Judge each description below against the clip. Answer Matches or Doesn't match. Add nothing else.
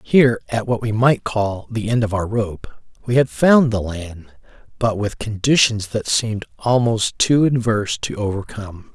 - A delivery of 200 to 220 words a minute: Doesn't match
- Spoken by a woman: Doesn't match